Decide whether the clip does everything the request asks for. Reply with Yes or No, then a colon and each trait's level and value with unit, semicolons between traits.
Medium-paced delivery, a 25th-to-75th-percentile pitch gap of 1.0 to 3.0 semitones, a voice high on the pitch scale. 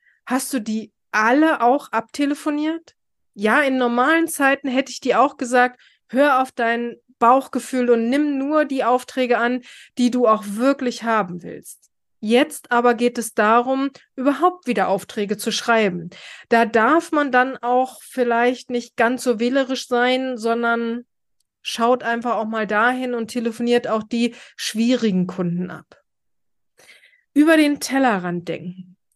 Yes: average, 140 wpm; average, 2.7 semitones; high, 245 Hz